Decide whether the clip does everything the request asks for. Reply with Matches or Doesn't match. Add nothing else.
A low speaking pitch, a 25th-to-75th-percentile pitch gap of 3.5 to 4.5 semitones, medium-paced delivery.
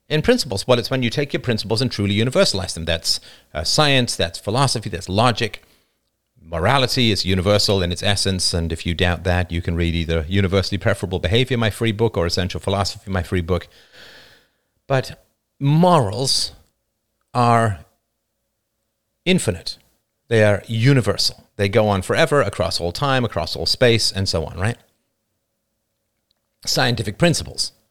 Matches